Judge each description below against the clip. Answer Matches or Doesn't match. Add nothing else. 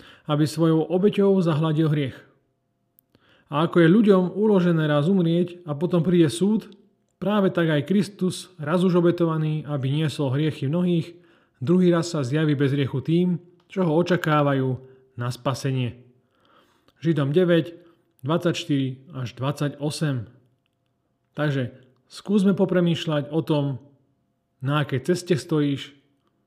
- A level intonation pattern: Doesn't match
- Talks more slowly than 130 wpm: Matches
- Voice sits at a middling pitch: Matches